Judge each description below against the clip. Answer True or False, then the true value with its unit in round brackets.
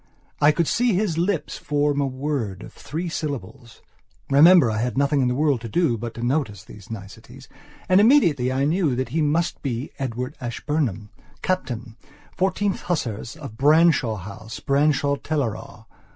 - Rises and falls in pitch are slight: False (5.2 semitones)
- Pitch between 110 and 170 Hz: True (140 Hz)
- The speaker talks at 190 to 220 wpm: False (150 wpm)